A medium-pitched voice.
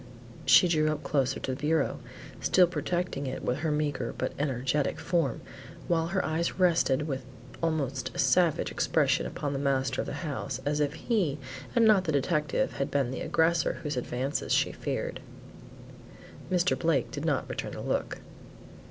Yes: medium, 150 Hz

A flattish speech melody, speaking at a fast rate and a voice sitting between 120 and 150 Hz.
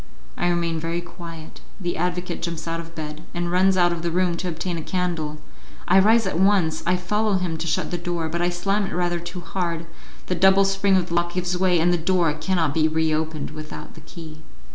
No: narrow, 1.9 semitones; fast, 225 wpm; medium, 175 Hz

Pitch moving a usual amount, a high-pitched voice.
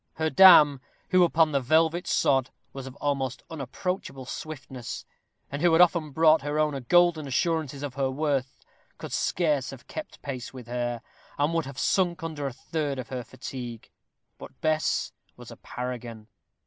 No: average, 3.7 semitones; medium, 145 Hz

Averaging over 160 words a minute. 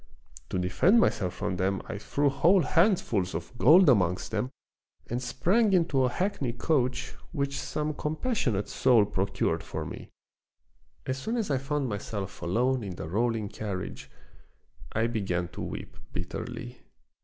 No: average, 145 wpm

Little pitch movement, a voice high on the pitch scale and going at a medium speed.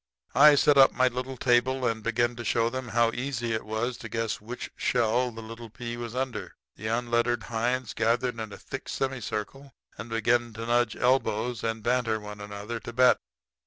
No: narrow, 1.9 semitones; low, 120 Hz; average, 190 wpm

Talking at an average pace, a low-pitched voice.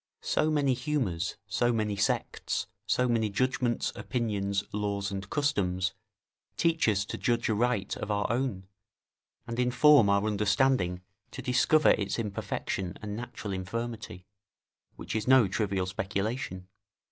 No: slow, 130 wpm; low, 110 Hz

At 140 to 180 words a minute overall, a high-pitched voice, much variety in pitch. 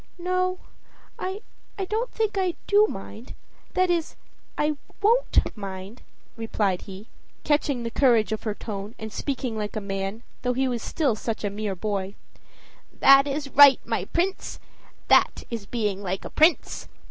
Yes: average, 155 wpm; high, 240 Hz; wide, 8.1 semitones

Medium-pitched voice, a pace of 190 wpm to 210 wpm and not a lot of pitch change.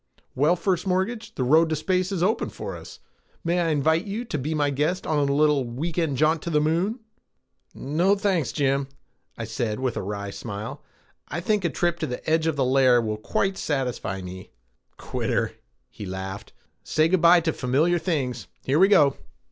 No: medium, 155 Hz; average, 200 wpm; wide, 5.4 semitones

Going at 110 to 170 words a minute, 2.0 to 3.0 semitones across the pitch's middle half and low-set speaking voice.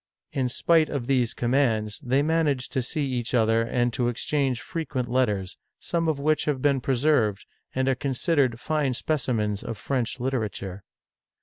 No: average, 160 wpm; average, 3.4 semitones; low, 130 Hz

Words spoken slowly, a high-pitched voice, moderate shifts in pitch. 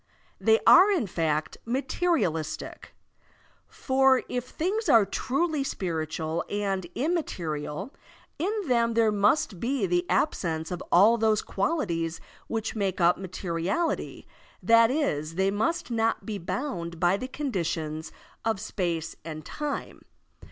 No: slow, 125 wpm; high, 205 Hz; wide, 7.5 semitones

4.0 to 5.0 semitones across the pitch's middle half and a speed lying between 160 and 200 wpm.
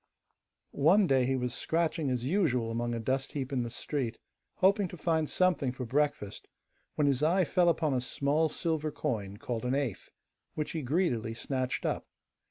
Yes: average, 4.4 semitones; average, 180 wpm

